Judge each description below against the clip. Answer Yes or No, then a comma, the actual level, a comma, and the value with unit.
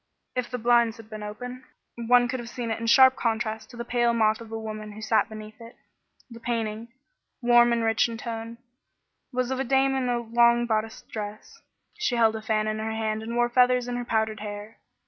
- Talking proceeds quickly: Yes, fast, 220 wpm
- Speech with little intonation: Yes, narrow, 1.7 semitones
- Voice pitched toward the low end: No, high, 230 Hz